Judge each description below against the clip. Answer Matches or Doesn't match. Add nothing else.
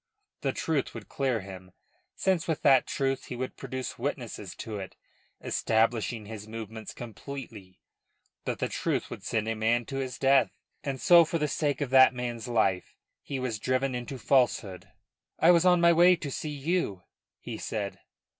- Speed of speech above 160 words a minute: Matches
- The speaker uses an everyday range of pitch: Matches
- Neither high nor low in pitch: Doesn't match